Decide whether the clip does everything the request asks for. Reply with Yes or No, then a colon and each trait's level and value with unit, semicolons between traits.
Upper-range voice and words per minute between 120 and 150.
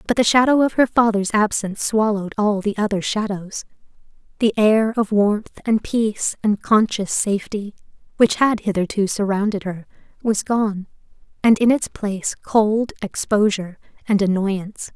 Yes: high, 210 Hz; average, 145 wpm